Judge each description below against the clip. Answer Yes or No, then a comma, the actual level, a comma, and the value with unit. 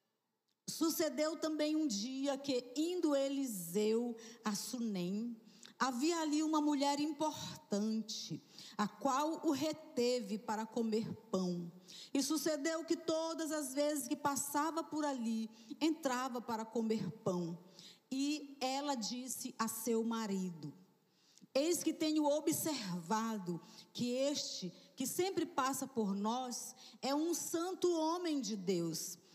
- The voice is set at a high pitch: Yes, very high, 255 Hz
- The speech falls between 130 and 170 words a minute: No, slow, 120 wpm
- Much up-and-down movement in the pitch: Yes, wide, 5.9 semitones